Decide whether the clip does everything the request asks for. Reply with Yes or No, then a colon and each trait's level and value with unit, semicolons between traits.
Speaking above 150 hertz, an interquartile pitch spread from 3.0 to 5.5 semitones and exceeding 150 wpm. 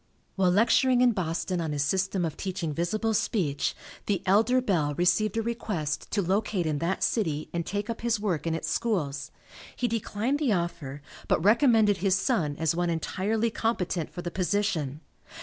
Yes: high, 190 Hz; average, 5.1 semitones; average, 175 wpm